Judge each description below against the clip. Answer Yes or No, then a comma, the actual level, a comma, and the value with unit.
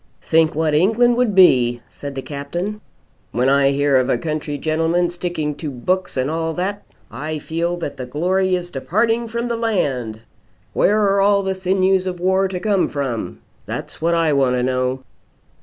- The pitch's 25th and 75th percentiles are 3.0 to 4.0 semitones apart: No, average, 5.3 semitones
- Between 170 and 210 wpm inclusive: Yes, average, 175 wpm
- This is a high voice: No, medium, 165 Hz